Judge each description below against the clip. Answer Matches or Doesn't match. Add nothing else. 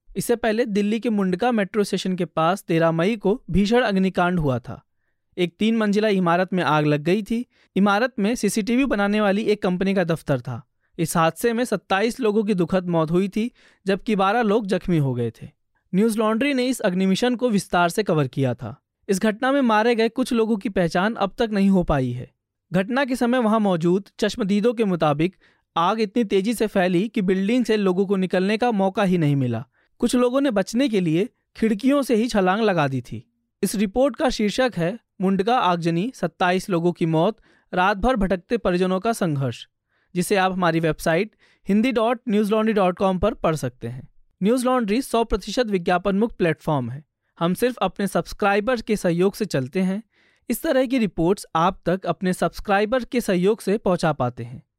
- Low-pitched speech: Doesn't match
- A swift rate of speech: Matches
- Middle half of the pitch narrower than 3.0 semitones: Doesn't match